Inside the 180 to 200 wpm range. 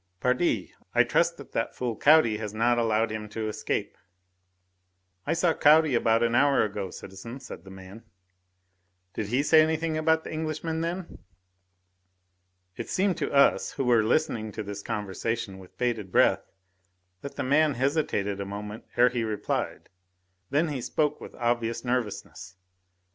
No: average, 155 wpm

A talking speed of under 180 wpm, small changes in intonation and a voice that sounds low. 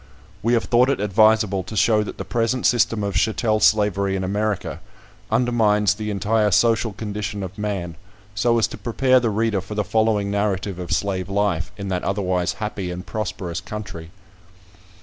Yes: average, 170 wpm; narrow, 2.2 semitones; low, 105 Hz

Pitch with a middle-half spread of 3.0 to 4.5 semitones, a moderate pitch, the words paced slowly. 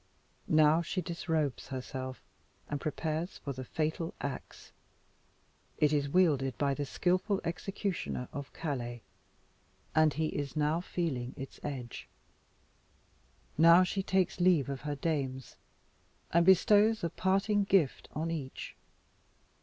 Yes: average, 4.2 semitones; medium, 155 Hz; slow, 120 wpm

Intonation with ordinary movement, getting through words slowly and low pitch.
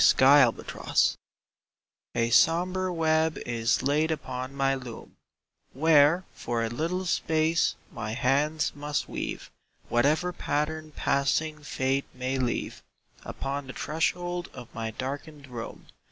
No: average, 3.7 semitones; slow, 110 wpm; medium, 145 Hz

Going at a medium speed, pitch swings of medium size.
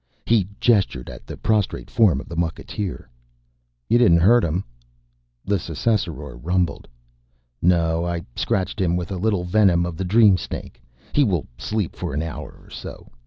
Yes: average, 165 wpm; average, 3.8 semitones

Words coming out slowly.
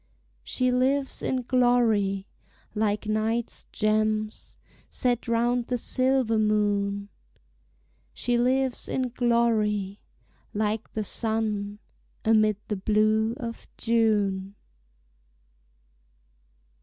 Yes: slow, 85 wpm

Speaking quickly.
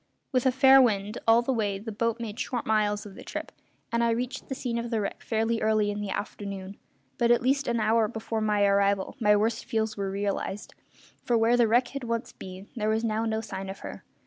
Yes: fast, 230 wpm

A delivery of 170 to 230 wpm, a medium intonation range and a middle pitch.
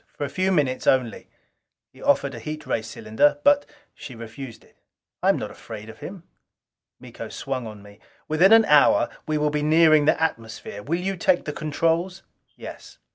No: average, 185 wpm; wide, 6.2 semitones; medium, 150 Hz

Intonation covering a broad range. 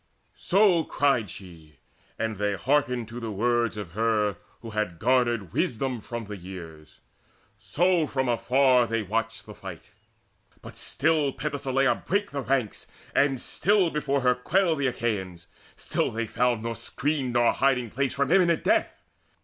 No: average, 4.5 semitones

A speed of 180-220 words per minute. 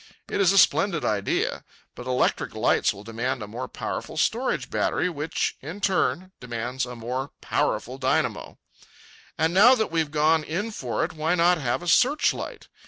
No: average, 170 wpm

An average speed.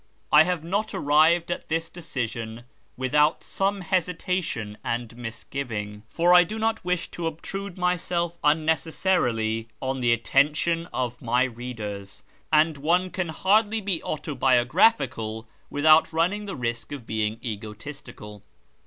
No: slow, 125 wpm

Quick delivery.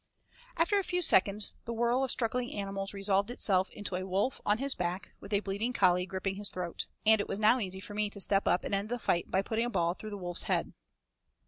Yes: fast, 240 wpm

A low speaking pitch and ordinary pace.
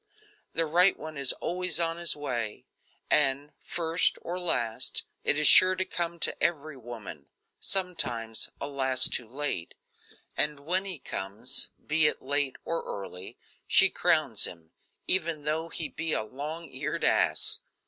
No: medium, 150 Hz; average, 145 wpm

